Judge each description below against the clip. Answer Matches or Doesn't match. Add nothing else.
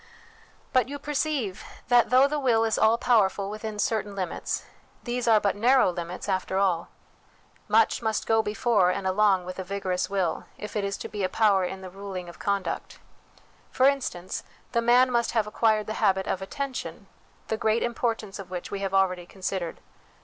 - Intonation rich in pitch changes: Doesn't match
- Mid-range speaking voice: Doesn't match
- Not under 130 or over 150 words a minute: Doesn't match